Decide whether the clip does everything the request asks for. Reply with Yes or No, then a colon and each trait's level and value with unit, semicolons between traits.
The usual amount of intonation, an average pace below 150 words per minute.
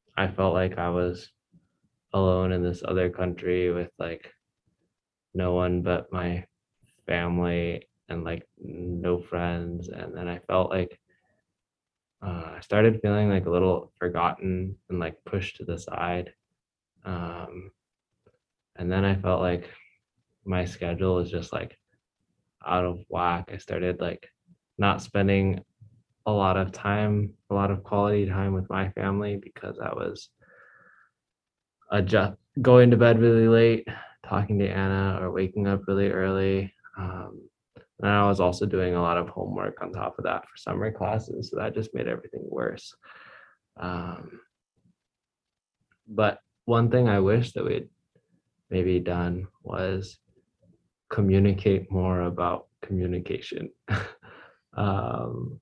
No: narrow, 2.1 semitones; slow, 135 wpm